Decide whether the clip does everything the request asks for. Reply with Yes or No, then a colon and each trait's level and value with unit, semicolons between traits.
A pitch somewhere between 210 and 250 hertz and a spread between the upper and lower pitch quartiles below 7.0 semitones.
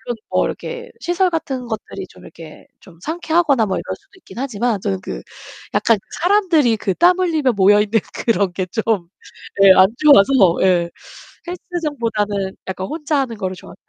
No: high, 230 Hz; wide, 8.6 semitones